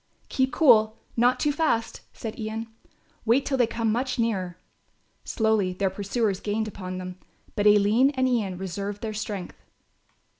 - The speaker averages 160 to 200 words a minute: No, average, 150 wpm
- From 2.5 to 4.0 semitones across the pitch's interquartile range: Yes, average, 3.1 semitones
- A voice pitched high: Yes, high, 220 Hz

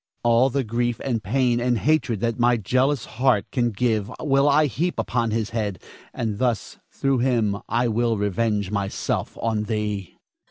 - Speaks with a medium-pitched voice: No, low, 115 Hz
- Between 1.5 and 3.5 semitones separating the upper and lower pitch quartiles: Yes, average, 2.9 semitones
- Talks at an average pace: Yes, average, 165 wpm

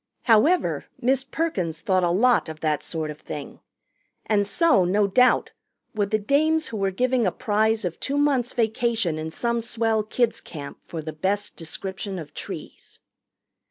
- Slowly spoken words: No, average, 165 wpm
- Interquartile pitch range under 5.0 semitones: No, wide, 5.6 semitones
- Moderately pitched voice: No, high, 210 Hz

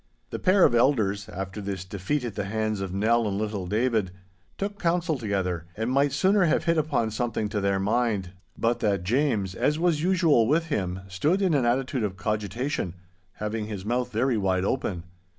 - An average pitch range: No, wide, 6.2 semitones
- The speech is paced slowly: No, average, 185 wpm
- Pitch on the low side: Yes, low, 110 Hz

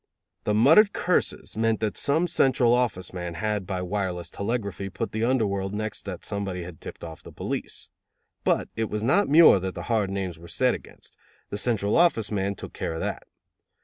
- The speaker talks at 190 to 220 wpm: Yes, average, 195 wpm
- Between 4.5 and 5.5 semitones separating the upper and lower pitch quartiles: No, average, 3.6 semitones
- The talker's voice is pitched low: Yes, low, 105 Hz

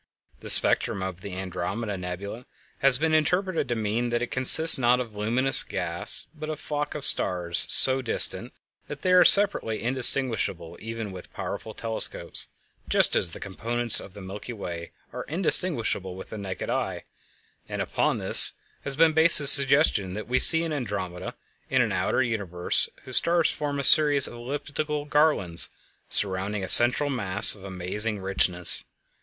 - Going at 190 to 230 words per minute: No, average, 170 wpm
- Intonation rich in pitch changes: Yes, wide, 7.1 semitones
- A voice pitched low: Yes, low, 115 Hz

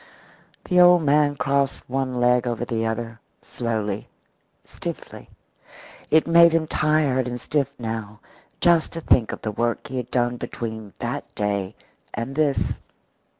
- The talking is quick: No, average, 145 wpm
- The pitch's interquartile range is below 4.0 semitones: No, average, 4.7 semitones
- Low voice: Yes, low, 125 Hz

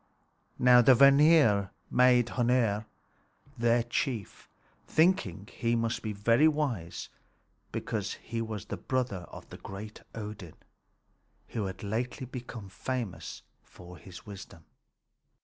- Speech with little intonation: No, average, 3.8 semitones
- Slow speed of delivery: Yes, slow, 115 wpm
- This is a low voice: Yes, low, 115 Hz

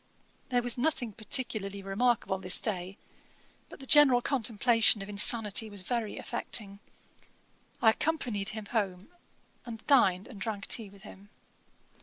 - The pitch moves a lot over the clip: No, average, 3.6 semitones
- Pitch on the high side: Yes, high, 220 Hz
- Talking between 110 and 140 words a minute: Yes, slow, 135 wpm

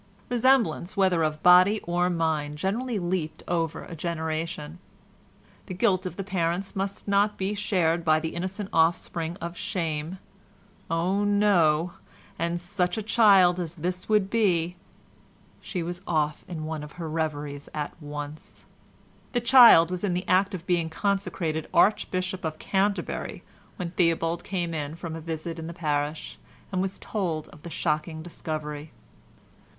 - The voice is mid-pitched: Yes, medium, 175 Hz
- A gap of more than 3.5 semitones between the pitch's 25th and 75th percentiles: No, average, 3.2 semitones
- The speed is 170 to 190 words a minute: No, average, 145 wpm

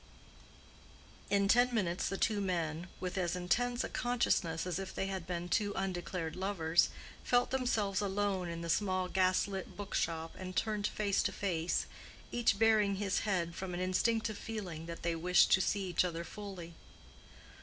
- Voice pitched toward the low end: No, high, 190 Hz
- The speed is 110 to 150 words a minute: No, average, 170 wpm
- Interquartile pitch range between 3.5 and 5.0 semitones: No, average, 2.9 semitones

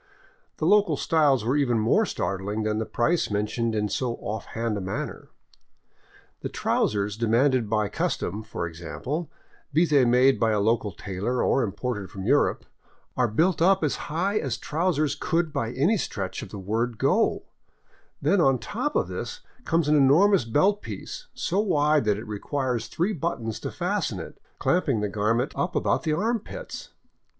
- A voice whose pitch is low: Yes, low, 125 Hz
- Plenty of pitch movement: Yes, wide, 7.1 semitones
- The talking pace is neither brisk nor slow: Yes, average, 170 wpm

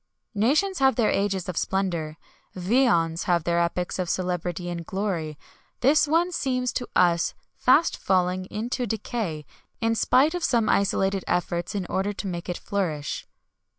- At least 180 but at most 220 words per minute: No, average, 150 wpm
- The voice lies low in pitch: No, high, 190 Hz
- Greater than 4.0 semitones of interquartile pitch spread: Yes, wide, 5.6 semitones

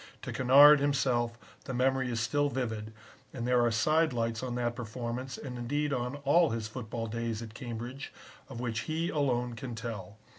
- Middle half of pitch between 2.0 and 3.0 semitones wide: Yes, narrow, 2.4 semitones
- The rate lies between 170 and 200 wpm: Yes, average, 180 wpm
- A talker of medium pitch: No, low, 120 Hz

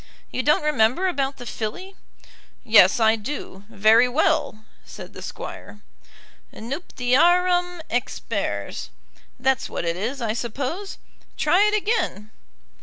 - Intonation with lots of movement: Yes, wide, 7.7 semitones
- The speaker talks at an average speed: No, slow, 115 wpm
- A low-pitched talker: No, very high, 255 Hz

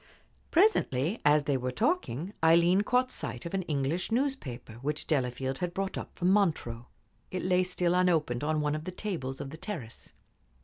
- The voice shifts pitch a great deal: Yes, wide, 5.7 semitones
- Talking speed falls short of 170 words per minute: No, average, 175 wpm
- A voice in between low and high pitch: Yes, medium, 165 Hz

